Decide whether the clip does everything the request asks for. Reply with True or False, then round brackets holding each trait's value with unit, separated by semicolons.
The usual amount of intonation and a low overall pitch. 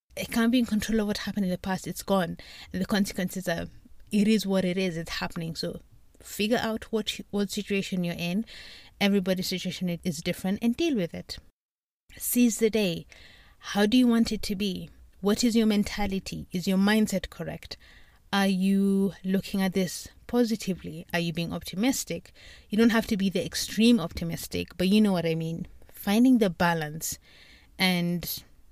False (3.4 semitones; 195 Hz)